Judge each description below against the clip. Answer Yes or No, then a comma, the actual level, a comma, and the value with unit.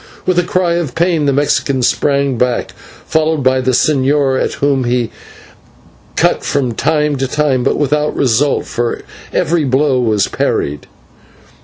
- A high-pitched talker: No, medium, 140 Hz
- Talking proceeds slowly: No, average, 150 wpm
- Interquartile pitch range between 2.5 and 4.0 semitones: Yes, average, 2.9 semitones